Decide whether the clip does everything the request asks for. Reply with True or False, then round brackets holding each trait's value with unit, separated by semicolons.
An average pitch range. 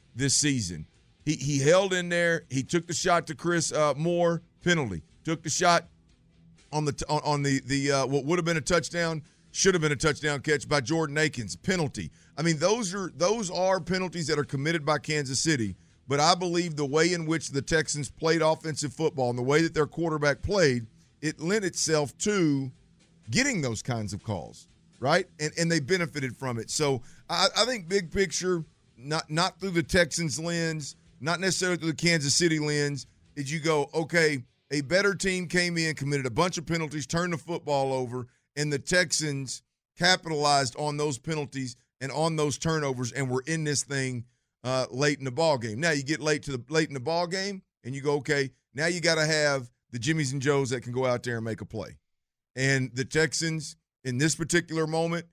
True (3.6 semitones)